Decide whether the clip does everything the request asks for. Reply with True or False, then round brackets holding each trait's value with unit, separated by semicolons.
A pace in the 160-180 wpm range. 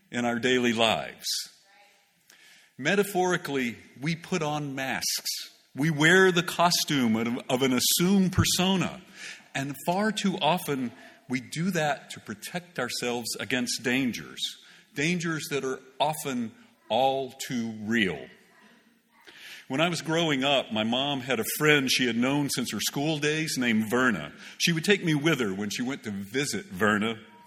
False (150 wpm)